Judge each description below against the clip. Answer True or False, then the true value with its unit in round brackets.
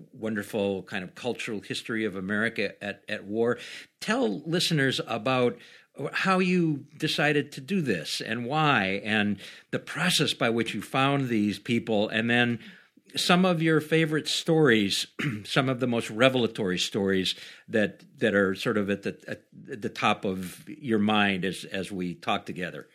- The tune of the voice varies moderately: False (6.5 semitones)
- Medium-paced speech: True (160 wpm)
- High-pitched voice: False (120 Hz)